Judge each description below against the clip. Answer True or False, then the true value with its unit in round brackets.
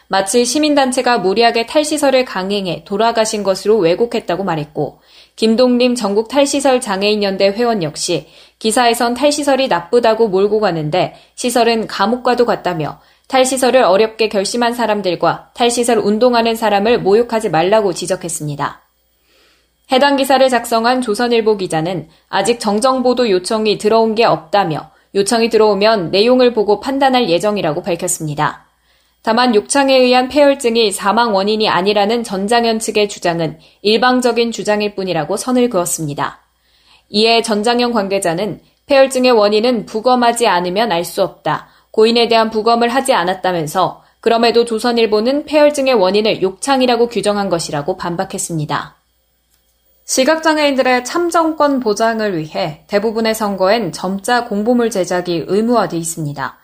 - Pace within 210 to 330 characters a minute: False (350 characters per minute)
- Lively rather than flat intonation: False (4.4 semitones)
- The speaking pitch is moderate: False (220 Hz)